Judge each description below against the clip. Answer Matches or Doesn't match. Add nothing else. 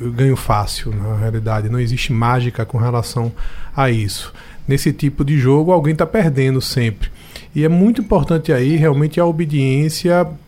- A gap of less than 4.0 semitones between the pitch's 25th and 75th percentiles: Doesn't match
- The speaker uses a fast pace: Doesn't match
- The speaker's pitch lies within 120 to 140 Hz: Matches